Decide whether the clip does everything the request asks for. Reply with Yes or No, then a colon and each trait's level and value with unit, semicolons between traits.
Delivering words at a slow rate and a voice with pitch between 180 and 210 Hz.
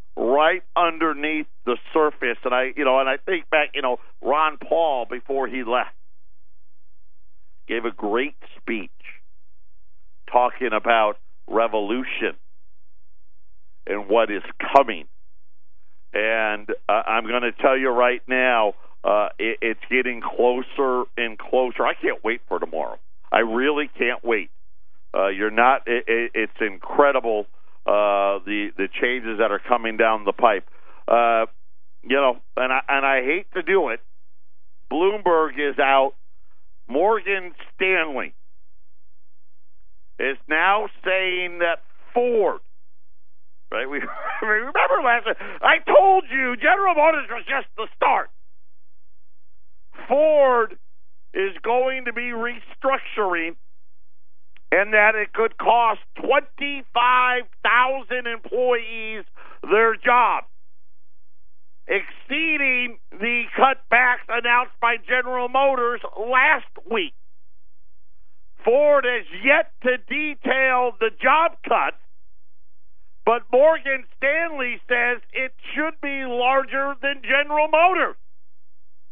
Yes: slow, 115 wpm; high, 190 Hz